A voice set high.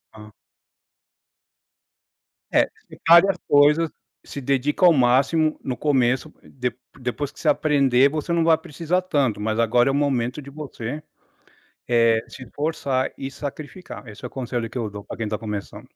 No: low, 135 Hz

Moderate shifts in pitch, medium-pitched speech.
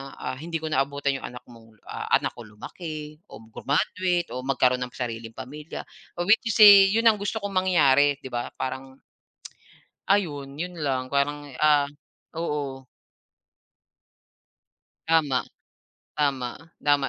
Yes: average, 4.0 semitones; medium, 145 Hz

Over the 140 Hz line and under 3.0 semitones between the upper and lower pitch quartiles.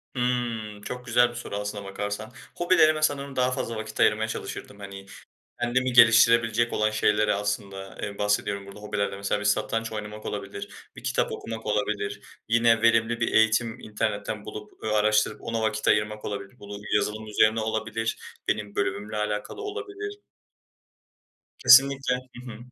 No: low, 110 Hz; narrow, 2.4 semitones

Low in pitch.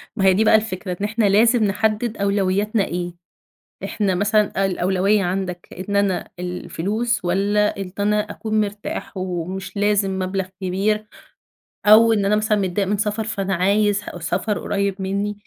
No: high, 200 Hz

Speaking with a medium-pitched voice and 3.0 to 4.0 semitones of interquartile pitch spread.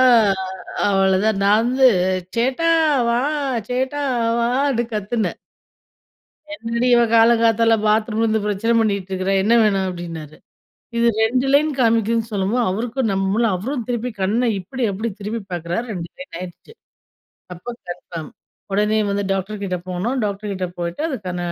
No: high, 215 Hz; average, 3.7 semitones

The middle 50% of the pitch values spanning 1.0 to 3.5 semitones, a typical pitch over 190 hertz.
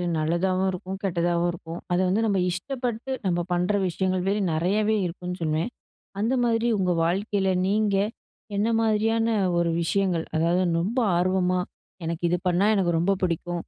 No: average, 2.9 semitones; medium, 185 Hz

